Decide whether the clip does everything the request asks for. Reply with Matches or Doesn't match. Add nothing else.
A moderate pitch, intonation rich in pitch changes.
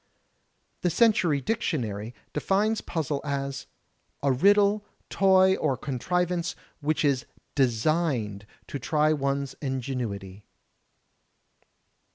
Matches